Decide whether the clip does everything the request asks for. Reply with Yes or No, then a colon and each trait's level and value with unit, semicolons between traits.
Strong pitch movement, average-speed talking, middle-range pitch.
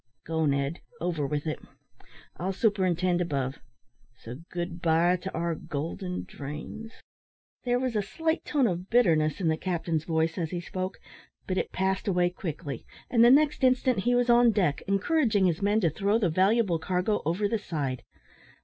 No: average, 4.8 semitones; average, 170 wpm; medium, 180 Hz